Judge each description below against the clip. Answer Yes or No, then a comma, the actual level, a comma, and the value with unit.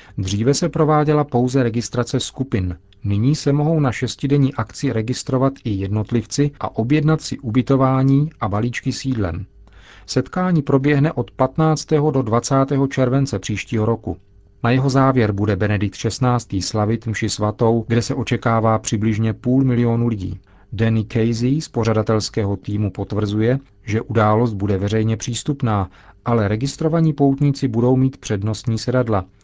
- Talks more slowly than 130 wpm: No, average, 135 wpm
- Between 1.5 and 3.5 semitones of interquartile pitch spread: No, average, 4.1 semitones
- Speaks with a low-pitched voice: Yes, low, 120 Hz